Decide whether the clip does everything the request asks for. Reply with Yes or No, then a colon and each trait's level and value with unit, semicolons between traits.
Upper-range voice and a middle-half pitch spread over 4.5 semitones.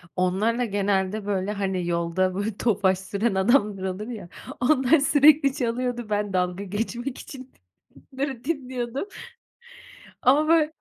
Yes: high, 215 Hz; average, 5.2 semitones